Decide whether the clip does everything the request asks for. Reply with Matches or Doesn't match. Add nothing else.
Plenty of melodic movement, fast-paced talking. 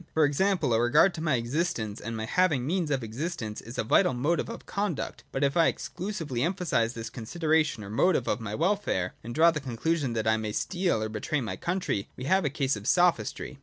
Matches